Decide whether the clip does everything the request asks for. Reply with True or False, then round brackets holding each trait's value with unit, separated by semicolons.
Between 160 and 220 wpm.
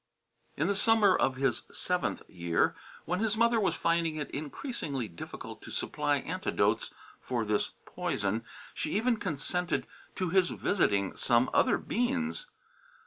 False (140 wpm)